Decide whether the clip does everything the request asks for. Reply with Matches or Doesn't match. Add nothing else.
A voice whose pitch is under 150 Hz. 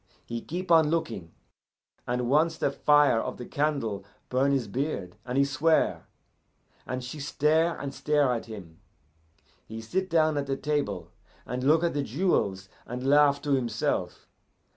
Matches